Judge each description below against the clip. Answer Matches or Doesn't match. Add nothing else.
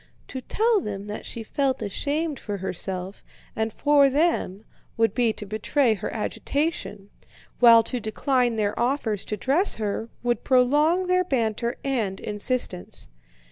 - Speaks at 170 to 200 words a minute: Doesn't match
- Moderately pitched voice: Doesn't match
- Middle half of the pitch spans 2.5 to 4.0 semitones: Doesn't match